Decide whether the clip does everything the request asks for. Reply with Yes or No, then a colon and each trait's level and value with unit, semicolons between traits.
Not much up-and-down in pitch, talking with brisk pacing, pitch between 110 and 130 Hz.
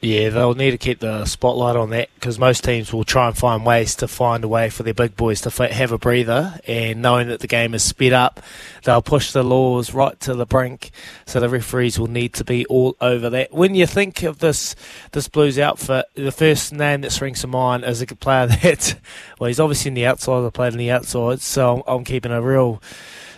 Yes: narrow, 1.7 semitones; fast, 235 wpm; low, 125 Hz